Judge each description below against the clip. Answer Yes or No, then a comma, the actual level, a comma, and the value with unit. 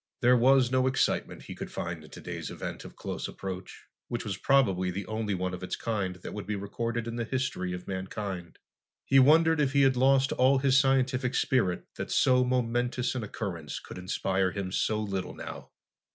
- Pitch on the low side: Yes, low, 115 Hz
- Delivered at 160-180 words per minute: No, average, 195 wpm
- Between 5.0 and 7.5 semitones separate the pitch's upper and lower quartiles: Yes, wide, 5.6 semitones